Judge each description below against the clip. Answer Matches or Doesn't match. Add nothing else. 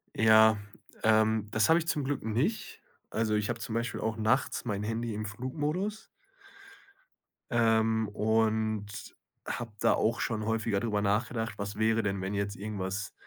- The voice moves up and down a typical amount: Doesn't match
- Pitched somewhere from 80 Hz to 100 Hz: Doesn't match